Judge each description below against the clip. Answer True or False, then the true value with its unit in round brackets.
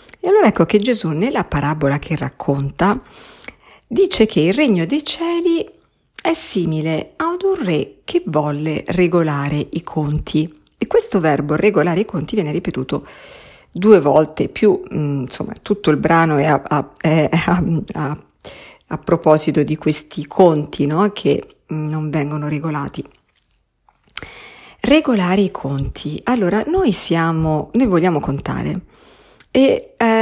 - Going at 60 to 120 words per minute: False (135 wpm)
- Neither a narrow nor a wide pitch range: False (6.5 semitones)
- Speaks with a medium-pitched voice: True (165 Hz)